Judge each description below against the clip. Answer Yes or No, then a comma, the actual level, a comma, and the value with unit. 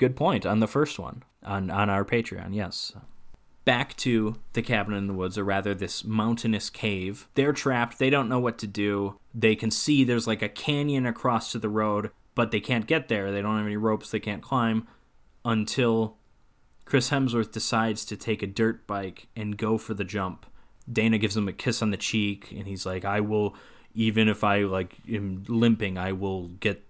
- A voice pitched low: Yes, low, 110 Hz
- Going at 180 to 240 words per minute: Yes, fast, 205 wpm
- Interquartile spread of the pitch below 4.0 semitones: Yes, narrow, 2.4 semitones